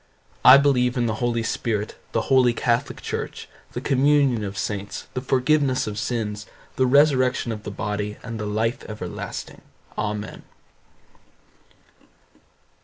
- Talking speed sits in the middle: No, slow, 130 wpm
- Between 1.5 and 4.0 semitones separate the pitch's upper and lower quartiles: Yes, average, 3.5 semitones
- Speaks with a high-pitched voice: No, low, 115 Hz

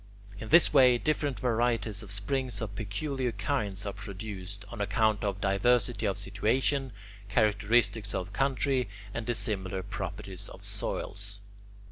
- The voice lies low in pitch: Yes, low, 105 Hz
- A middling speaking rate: No, slow, 130 wpm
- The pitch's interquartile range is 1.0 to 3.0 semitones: No, average, 3.6 semitones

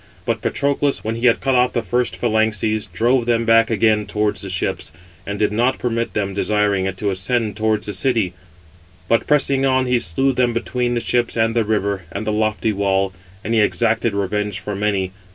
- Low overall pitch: Yes, low, 110 Hz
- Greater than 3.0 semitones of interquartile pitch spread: No, average, 2.7 semitones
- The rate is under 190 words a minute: No, average, 200 wpm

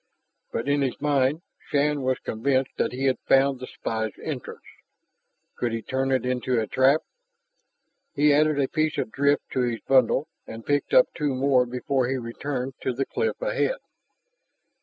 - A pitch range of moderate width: No, narrow, 2.3 semitones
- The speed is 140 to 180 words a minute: Yes, average, 170 wpm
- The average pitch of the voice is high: No, low, 135 Hz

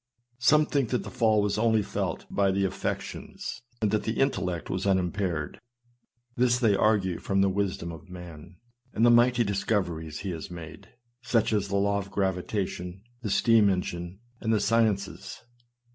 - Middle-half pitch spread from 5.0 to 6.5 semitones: No, average, 3.4 semitones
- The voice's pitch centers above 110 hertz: No, low, 100 Hz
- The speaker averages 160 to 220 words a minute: Yes, average, 165 wpm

